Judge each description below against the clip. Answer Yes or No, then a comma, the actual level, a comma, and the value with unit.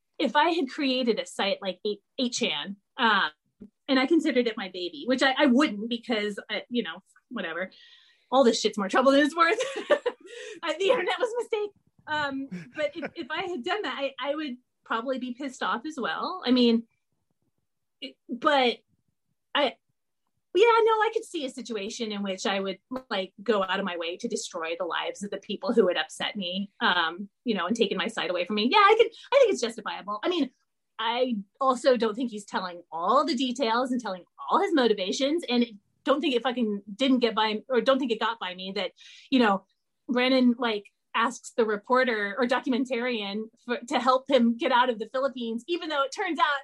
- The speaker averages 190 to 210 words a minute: Yes, fast, 205 wpm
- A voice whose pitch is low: No, very high, 250 Hz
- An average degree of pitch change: Yes, average, 4.7 semitones